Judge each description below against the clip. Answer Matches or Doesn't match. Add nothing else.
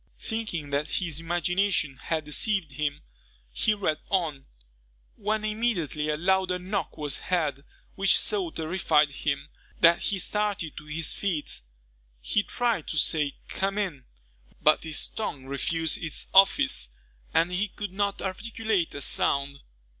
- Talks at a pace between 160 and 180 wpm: Doesn't match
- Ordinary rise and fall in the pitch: Matches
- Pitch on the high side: Doesn't match